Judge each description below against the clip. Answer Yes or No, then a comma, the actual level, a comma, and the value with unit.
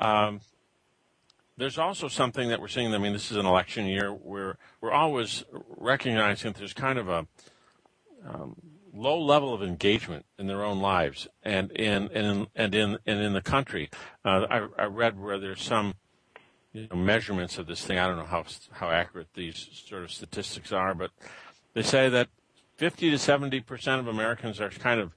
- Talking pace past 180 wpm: Yes, average, 190 wpm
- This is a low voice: Yes, low, 105 Hz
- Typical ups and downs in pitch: Yes, average, 3.9 semitones